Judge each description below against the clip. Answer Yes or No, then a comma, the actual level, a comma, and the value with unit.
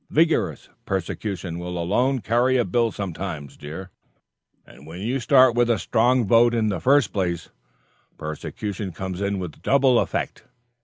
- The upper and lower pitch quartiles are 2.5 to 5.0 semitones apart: No, wide, 5.4 semitones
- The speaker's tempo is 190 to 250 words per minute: No, average, 150 wpm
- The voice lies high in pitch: No, low, 100 Hz